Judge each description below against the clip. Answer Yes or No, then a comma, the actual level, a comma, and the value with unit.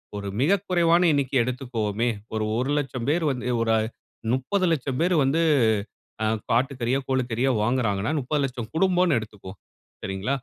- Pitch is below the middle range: Yes, low, 130 Hz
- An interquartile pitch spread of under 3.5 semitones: No, average, 4.8 semitones